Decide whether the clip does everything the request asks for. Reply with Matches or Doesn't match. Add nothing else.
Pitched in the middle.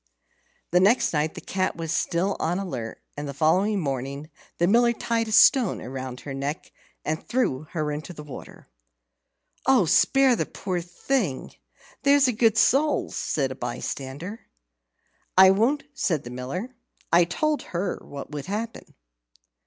Matches